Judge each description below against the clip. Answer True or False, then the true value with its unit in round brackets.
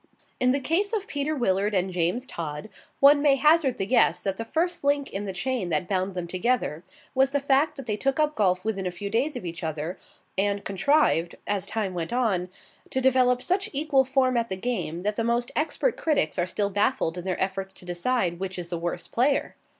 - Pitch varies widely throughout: True (6.7 semitones)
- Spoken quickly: True (220 wpm)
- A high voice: True (220 Hz)